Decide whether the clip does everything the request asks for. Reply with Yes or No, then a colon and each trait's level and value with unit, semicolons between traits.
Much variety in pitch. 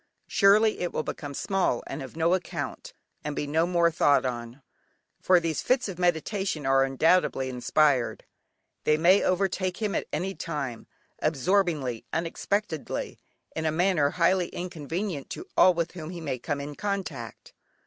No: average, 4.5 semitones